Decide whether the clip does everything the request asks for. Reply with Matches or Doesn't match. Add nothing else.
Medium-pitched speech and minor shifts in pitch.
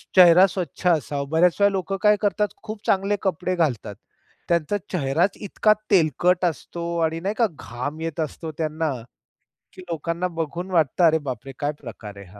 Doesn't match